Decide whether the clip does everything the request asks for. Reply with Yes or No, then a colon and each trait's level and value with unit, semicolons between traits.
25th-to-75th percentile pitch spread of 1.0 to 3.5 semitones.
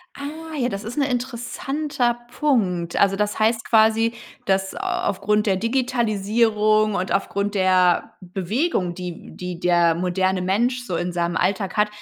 No: average, 4.5 semitones